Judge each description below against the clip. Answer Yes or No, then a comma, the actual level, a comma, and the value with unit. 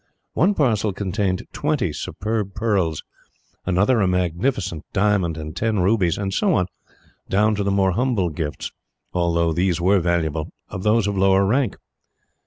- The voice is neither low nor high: No, very low, 95 Hz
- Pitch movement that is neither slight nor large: Yes, average, 3.3 semitones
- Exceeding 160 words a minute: No, average, 150 wpm